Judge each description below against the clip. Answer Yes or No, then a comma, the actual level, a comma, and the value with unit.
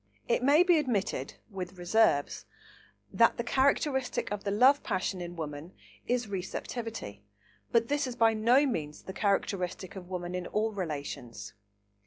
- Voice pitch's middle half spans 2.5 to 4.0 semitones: No, wide, 5.6 semitones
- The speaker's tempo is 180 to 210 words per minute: No, average, 150 wpm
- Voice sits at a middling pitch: No, high, 200 Hz